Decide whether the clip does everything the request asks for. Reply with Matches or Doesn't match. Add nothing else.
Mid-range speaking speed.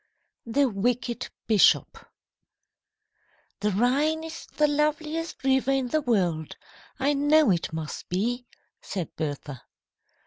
Doesn't match